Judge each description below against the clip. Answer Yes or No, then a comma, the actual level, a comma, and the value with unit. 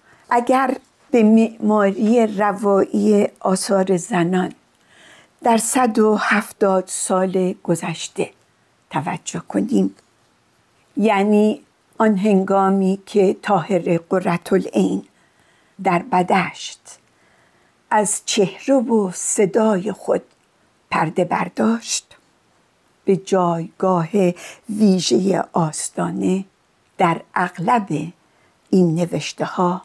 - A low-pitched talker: No, high, 195 Hz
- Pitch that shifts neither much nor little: Yes, average, 3.2 semitones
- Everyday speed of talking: No, slow, 80 wpm